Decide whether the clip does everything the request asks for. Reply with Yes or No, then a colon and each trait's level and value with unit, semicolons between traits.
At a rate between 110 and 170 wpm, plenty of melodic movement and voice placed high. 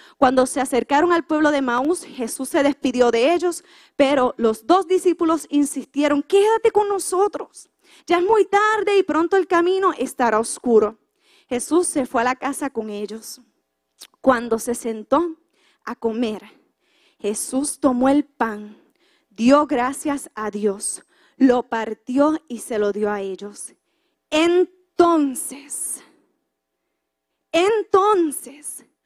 Yes: slow, 125 wpm; wide, 6.5 semitones; very high, 285 Hz